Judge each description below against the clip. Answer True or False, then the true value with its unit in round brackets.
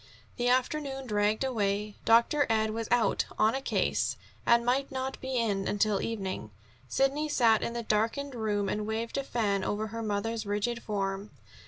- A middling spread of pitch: True (3.2 semitones)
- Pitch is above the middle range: True (225 Hz)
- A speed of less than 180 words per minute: True (170 wpm)